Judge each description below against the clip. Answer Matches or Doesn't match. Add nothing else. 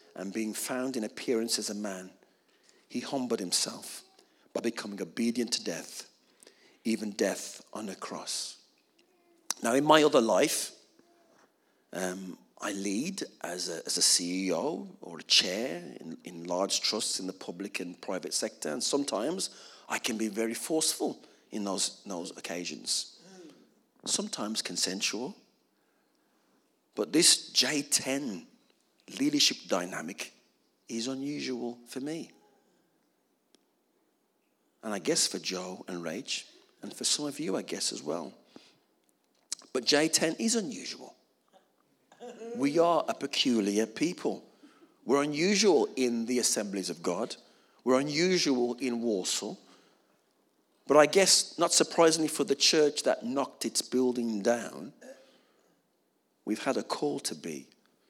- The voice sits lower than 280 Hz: Matches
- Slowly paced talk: Matches